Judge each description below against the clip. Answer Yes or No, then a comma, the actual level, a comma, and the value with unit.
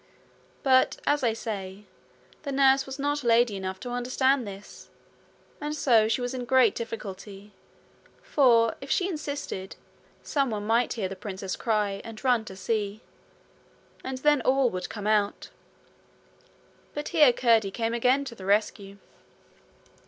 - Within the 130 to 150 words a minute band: Yes, average, 145 wpm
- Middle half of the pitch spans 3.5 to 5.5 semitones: Yes, average, 4.4 semitones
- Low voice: No, high, 230 Hz